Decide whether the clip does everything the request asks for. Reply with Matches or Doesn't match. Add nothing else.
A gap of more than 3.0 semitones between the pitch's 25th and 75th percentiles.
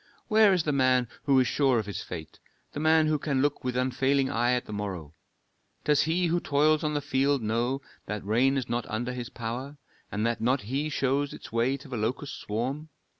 Matches